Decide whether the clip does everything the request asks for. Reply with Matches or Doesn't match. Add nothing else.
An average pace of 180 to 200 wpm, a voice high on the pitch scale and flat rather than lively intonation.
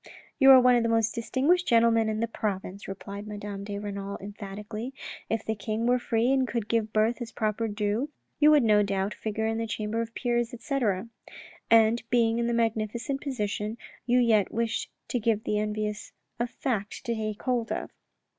Matches